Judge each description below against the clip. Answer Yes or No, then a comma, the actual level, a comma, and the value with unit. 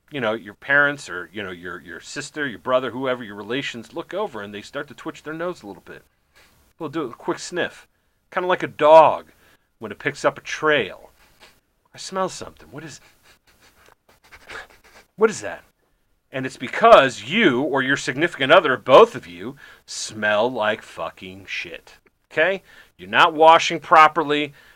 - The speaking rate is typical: Yes, average, 170 wpm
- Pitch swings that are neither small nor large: No, wide, 6.8 semitones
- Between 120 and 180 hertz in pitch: Yes, medium, 140 Hz